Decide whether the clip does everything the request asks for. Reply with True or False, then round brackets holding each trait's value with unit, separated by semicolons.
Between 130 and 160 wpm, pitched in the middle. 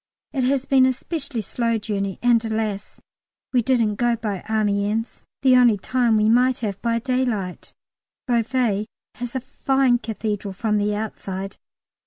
False (150 wpm; 230 Hz)